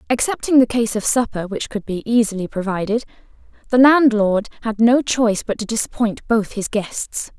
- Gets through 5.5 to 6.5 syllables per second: No, 5.1 syllables/s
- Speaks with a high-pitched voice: Yes, high, 225 Hz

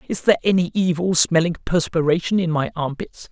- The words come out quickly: No, average, 165 wpm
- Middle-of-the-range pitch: Yes, medium, 170 Hz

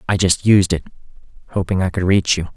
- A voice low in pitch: Yes, very low, 95 Hz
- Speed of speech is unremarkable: No, fast, 210 wpm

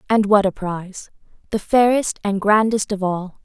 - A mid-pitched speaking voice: No, high, 205 Hz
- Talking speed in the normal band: Yes, average, 175 wpm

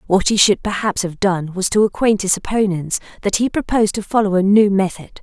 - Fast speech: Yes, fast, 220 wpm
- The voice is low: No, high, 200 Hz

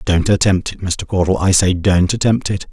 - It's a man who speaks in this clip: Yes, male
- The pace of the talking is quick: Yes, fast, 220 wpm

